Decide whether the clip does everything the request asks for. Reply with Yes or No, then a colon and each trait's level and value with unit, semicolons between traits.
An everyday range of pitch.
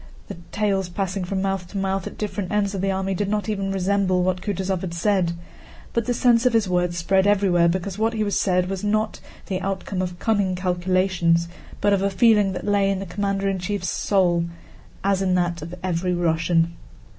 No: narrow, 2.0 semitones